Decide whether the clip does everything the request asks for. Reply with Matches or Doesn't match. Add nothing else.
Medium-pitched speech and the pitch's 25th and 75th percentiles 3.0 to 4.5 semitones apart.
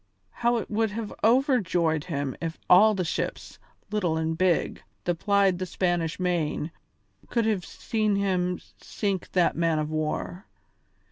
Matches